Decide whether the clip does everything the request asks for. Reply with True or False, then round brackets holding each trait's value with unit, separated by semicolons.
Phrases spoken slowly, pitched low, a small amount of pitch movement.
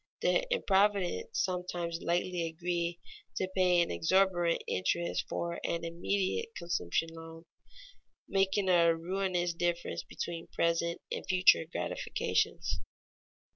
False (105 wpm; 175 Hz; 2.1 semitones)